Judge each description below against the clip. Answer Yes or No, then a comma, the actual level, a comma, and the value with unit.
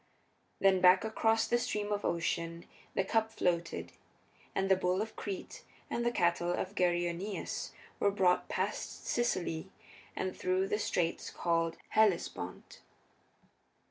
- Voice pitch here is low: No, high, 190 Hz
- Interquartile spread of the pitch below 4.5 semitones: Yes, average, 3.2 semitones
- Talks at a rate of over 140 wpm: No, slow, 135 wpm